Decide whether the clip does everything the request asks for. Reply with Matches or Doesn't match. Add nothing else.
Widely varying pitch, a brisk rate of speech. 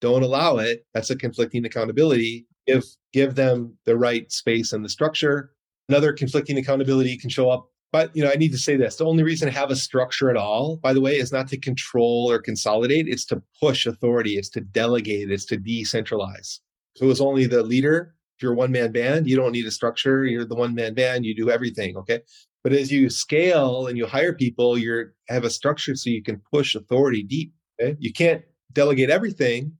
Doesn't match